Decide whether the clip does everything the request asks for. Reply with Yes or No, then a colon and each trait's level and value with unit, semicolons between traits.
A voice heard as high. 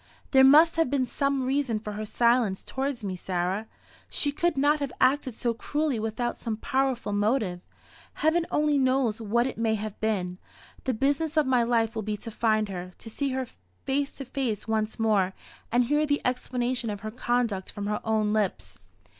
Yes: high, 240 Hz